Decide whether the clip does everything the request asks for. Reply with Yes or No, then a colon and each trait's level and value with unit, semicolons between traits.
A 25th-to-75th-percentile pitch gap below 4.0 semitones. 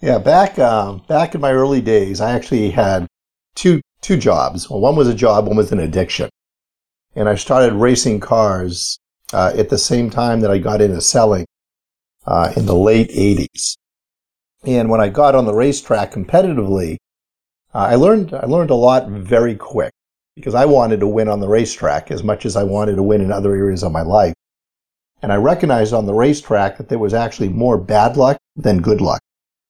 No: average, 4.3 semitones